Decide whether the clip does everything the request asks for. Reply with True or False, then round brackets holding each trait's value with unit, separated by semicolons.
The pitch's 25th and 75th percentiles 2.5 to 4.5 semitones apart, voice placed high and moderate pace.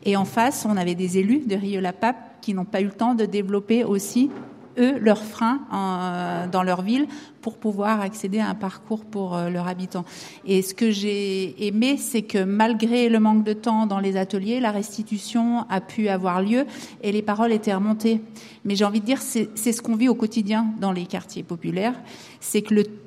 True (2.9 semitones; 215 Hz; 205 wpm)